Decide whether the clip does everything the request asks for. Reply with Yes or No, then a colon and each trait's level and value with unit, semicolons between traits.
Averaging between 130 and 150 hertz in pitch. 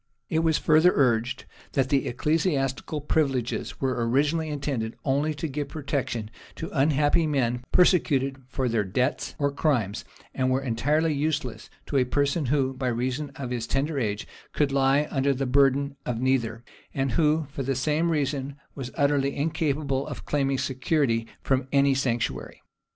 Yes: low, 135 Hz